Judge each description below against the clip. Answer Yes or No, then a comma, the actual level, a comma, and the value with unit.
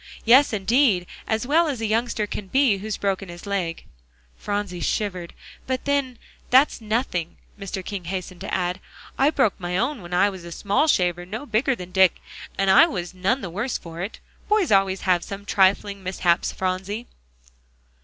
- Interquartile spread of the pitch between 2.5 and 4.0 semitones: No, average, 4.5 semitones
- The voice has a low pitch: No, high, 200 Hz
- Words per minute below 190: Yes, average, 180 wpm